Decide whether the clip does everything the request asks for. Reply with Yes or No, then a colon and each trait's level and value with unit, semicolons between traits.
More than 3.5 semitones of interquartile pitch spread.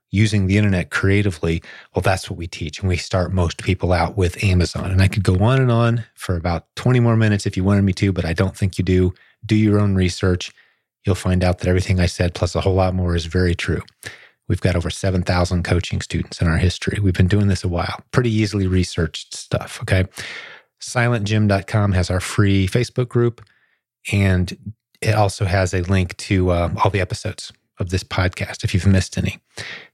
No: narrow, 2.6 semitones